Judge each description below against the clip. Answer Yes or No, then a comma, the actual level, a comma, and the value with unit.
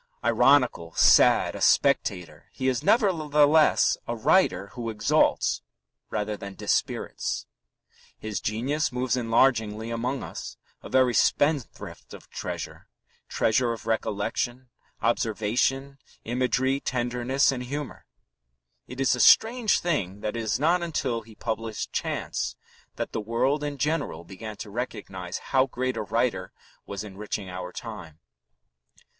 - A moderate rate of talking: No, slow, 125 wpm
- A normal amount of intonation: Yes, average, 4.0 semitones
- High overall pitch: No, low, 120 Hz